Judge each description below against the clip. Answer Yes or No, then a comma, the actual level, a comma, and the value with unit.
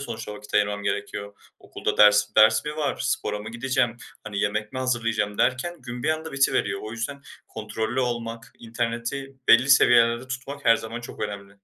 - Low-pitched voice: Yes, low, 115 Hz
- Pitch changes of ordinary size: Yes, average, 3.6 semitones